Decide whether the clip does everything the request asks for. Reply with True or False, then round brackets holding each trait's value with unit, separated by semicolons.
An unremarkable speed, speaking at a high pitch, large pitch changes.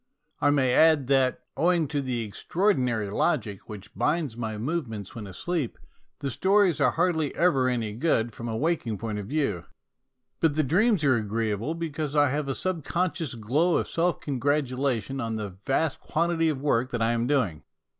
False (180 wpm; 135 Hz; 5.9 semitones)